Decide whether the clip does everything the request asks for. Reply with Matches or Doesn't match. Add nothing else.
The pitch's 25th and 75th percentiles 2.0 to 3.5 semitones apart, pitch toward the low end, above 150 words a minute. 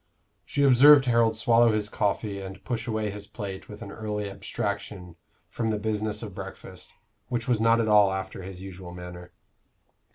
Matches